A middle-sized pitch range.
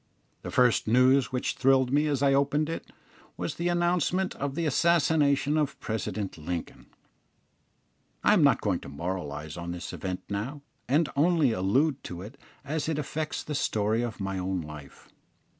No: wide, 7.7 semitones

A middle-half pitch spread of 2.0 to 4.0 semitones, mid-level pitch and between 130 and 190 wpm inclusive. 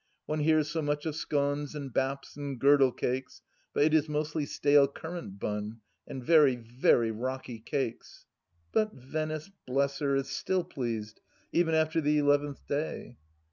Yes: average, 2.9 semitones; medium, 145 Hz; average, 160 wpm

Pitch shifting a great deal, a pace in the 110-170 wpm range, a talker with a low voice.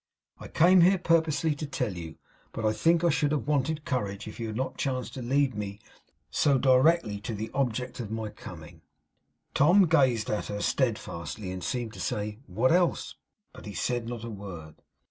No: wide, 5.7 semitones; average, 190 wpm; low, 120 Hz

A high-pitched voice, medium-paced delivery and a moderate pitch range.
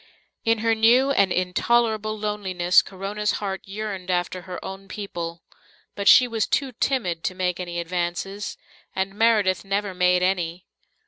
Yes: high, 195 Hz; average, 145 wpm; average, 3.0 semitones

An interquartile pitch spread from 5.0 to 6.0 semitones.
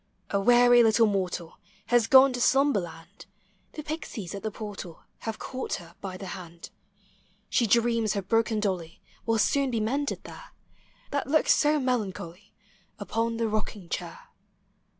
No: average, 4.2 semitones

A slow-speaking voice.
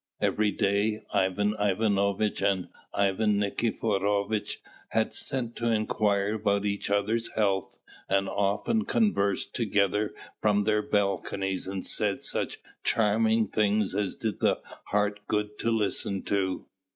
Yes: slow, 125 wpm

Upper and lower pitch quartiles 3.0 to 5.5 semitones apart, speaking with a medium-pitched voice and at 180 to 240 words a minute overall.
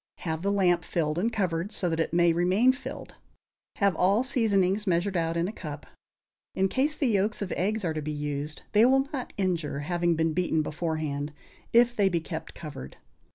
Yes: average, 4.2 semitones; medium, 175 Hz; average, 195 wpm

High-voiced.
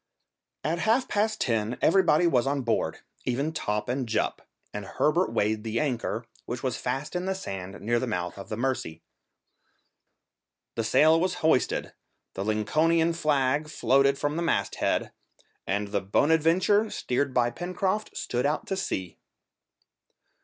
No: low, 135 Hz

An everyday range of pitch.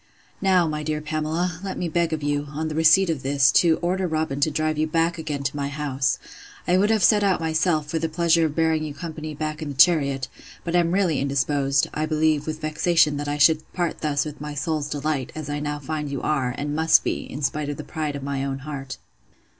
No: narrow, 2.1 semitones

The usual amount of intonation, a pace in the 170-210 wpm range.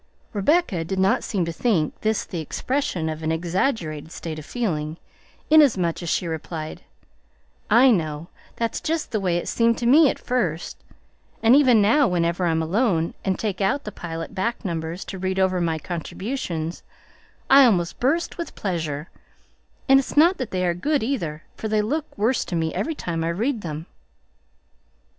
No: wide, 6.5 semitones; average, 175 wpm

